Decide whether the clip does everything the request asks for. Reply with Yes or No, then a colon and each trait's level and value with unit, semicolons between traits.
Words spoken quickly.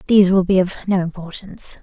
No: average, 195 wpm